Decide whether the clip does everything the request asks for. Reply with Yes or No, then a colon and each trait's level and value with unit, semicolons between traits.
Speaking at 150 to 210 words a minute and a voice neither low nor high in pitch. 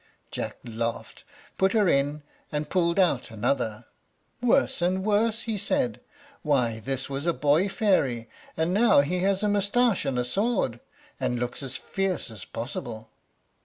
Yes: average, 155 wpm; medium, 150 Hz